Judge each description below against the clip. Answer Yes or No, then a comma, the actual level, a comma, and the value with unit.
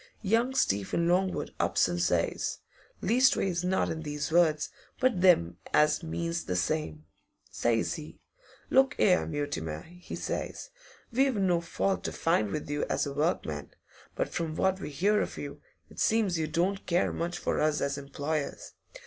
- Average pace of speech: Yes, average, 160 wpm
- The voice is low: No, medium, 165 Hz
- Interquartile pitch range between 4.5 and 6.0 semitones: Yes, average, 4.8 semitones